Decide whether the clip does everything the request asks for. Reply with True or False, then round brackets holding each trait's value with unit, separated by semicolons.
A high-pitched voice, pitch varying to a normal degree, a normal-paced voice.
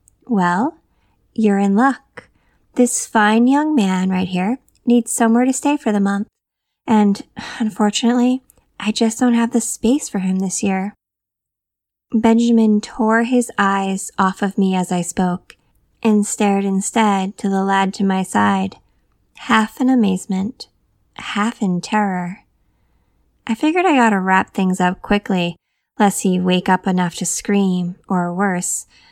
True (205 Hz; 3.5 semitones; 150 wpm)